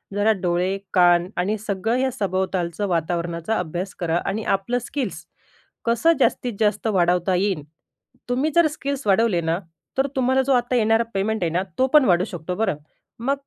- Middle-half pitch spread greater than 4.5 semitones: Yes, average, 5.3 semitones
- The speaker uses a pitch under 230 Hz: Yes, high, 200 Hz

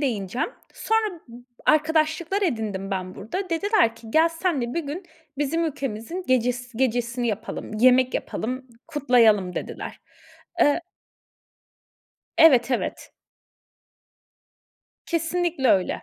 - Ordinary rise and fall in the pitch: No, wide, 6.1 semitones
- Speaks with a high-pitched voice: Yes, very high, 260 Hz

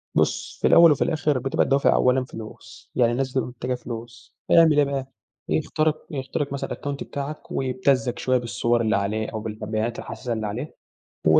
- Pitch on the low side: Yes, low, 125 Hz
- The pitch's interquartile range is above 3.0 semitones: Yes, average, 3.5 semitones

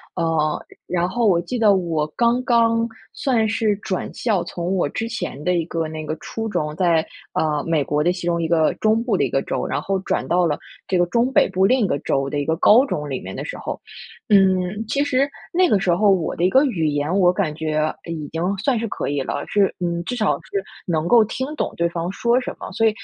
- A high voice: No, medium, 180 Hz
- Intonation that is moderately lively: No, wide, 5.7 semitones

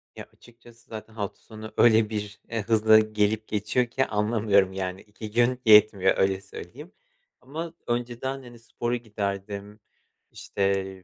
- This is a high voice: No, low, 110 Hz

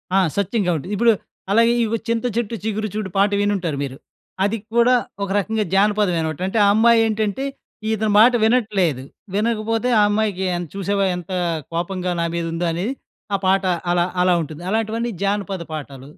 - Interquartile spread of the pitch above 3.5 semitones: Yes, average, 3.9 semitones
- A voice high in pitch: Yes, high, 200 Hz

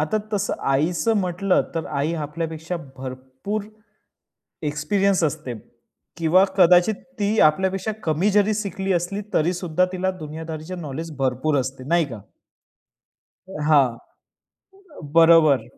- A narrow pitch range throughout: No, average, 4.0 semitones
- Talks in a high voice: No, medium, 165 Hz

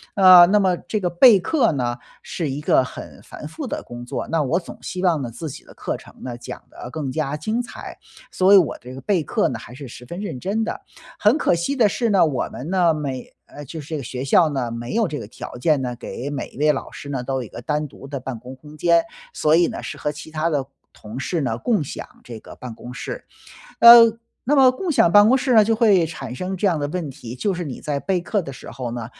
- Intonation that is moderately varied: No, wide, 6.5 semitones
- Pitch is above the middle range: No, medium, 155 Hz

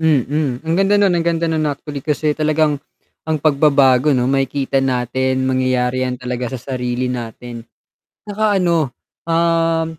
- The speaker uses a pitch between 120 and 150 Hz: Yes, medium, 140 Hz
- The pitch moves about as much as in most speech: Yes, average, 4.0 semitones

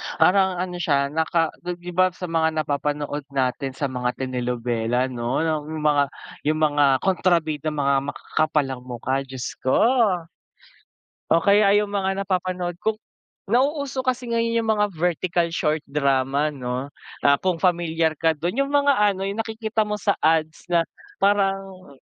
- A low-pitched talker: No, medium, 160 Hz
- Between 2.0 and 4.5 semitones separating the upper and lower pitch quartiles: No, wide, 5.5 semitones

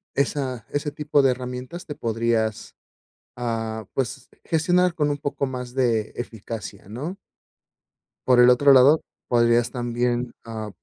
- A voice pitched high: No, low, 125 Hz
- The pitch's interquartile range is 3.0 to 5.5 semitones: Yes, average, 3.5 semitones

